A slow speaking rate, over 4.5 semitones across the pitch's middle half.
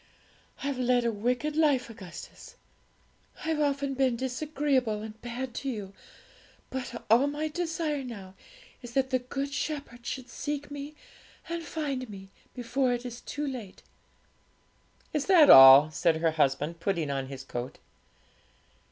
No: average, 145 wpm; wide, 5.5 semitones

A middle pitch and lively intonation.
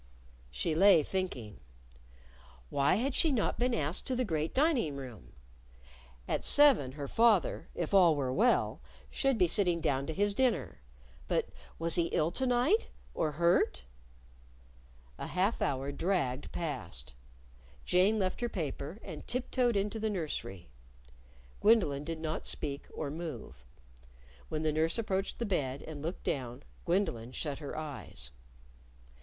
Yes: medium, 165 Hz; wide, 6.7 semitones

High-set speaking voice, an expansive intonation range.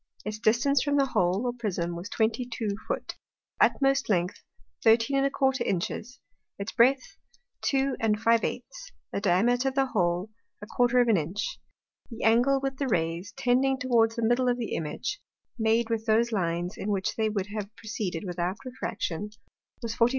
No: high, 225 Hz; average, 4.0 semitones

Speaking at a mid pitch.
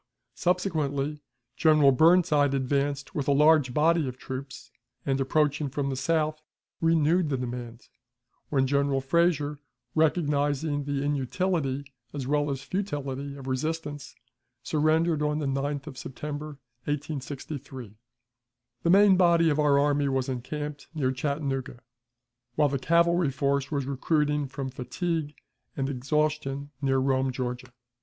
Yes: medium, 145 Hz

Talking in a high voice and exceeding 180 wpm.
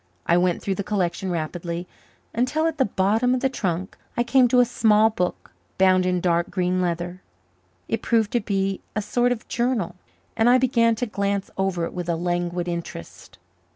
Yes: high, 195 Hz; average, 190 wpm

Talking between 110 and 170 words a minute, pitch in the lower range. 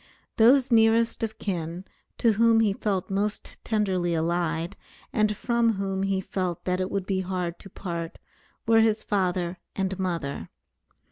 No: average, 150 wpm; high, 195 Hz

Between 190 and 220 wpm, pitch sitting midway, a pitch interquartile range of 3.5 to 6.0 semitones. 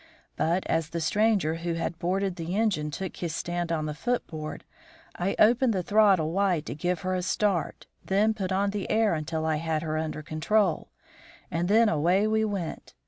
Yes: average, 195 wpm; medium, 175 Hz; average, 4.1 semitones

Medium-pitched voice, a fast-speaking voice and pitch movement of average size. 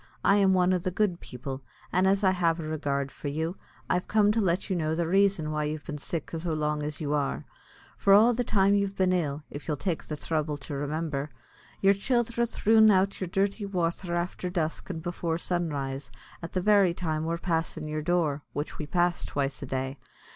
Yes: medium, 170 Hz; fast, 210 wpm; average, 4.1 semitones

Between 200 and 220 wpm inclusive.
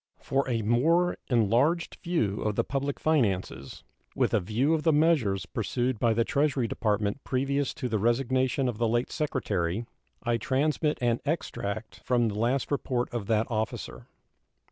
No: average, 160 wpm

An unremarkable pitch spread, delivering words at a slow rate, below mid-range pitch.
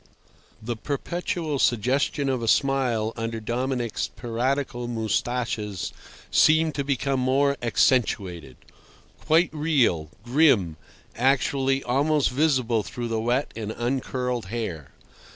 Yes: average, 3.5 semitones; slow, 100 wpm; low, 125 Hz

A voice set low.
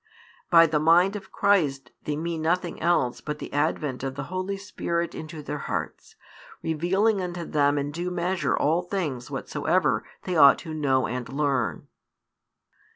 No: medium, 160 Hz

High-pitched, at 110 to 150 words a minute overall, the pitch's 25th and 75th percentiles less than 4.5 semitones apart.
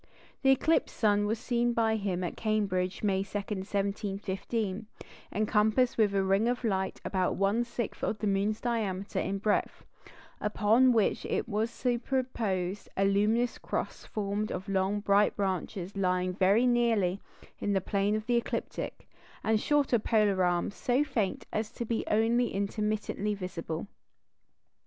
Yes: high, 210 Hz; average, 145 wpm; average, 2.7 semitones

